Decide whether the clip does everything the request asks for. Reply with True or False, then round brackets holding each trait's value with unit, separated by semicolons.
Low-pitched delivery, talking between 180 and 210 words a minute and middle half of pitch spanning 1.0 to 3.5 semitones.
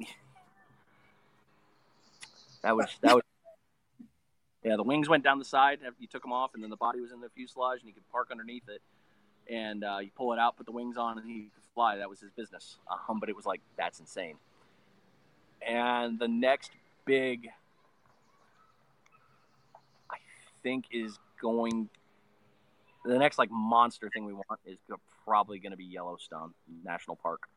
False (115 Hz; 170 wpm; 3.1 semitones)